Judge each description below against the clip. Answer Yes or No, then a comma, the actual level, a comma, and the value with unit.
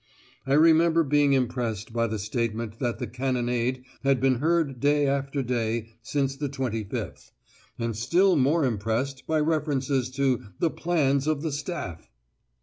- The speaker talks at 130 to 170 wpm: Yes, average, 145 wpm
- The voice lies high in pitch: No, low, 135 Hz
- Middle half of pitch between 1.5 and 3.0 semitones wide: No, average, 3.9 semitones